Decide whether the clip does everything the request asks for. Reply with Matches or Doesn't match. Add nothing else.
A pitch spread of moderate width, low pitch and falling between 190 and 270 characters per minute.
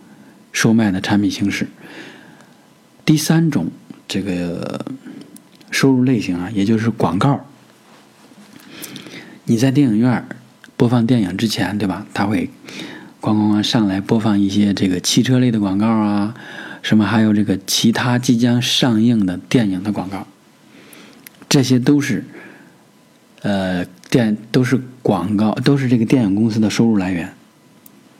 Matches